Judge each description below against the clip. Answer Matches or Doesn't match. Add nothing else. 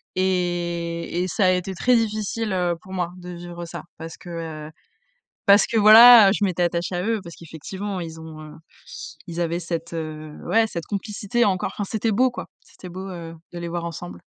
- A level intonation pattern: Doesn't match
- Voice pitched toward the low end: Doesn't match